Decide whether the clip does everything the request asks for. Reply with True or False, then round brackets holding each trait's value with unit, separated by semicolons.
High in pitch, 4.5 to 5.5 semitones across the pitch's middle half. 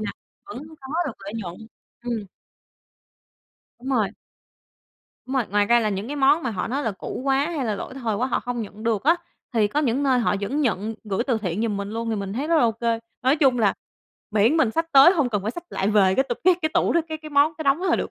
True (235 Hz; 4.8 semitones)